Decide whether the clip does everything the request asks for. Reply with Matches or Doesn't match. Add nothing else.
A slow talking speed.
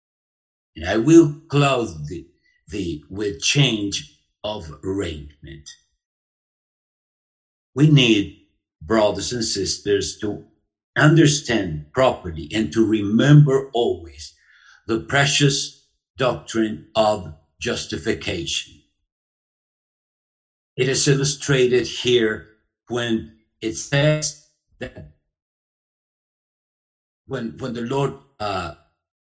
Matches